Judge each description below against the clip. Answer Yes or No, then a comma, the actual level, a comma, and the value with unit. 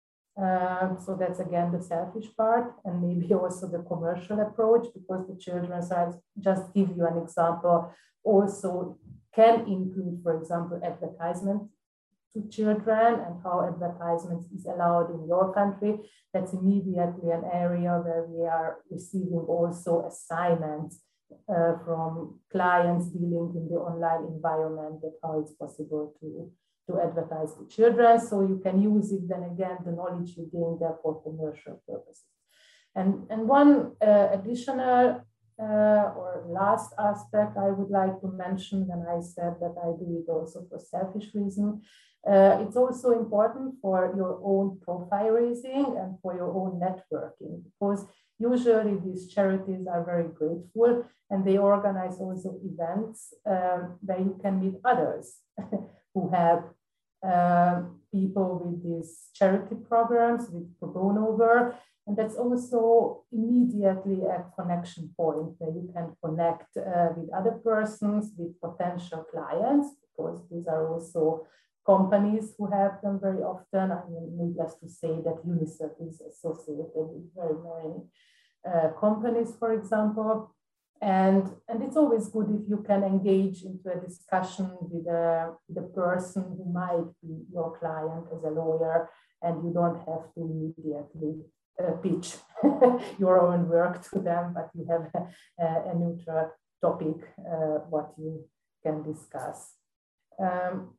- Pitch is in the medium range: Yes, medium, 180 Hz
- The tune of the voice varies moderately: Yes, average, 3.3 semitones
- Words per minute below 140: No, average, 145 wpm